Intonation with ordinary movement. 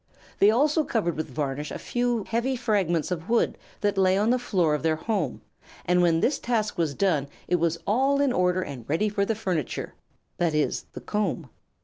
No: wide, 5.8 semitones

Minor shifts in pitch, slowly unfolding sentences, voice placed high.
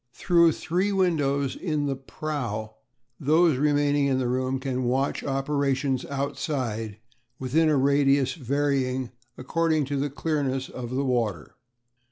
No: narrow, 2.3 semitones; slow, 130 wpm; medium, 140 Hz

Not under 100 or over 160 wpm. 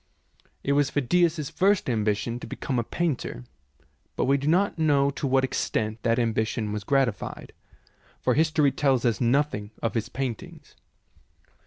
Yes: average, 150 wpm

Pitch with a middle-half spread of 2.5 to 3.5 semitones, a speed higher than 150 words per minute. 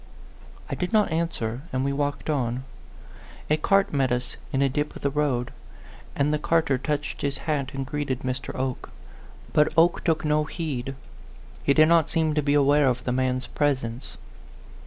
Yes: average, 2.8 semitones; average, 180 wpm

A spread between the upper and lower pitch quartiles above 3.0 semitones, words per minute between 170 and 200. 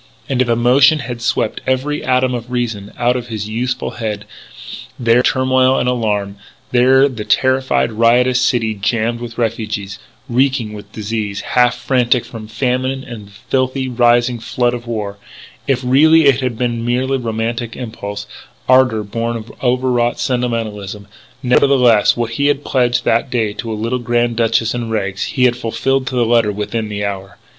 No: narrow, 2.4 semitones; average, 175 wpm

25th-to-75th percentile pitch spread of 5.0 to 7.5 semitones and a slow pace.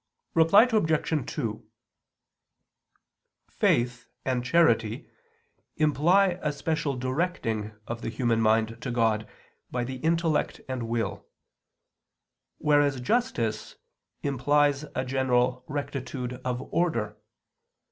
No: average, 4.5 semitones; slow, 95 wpm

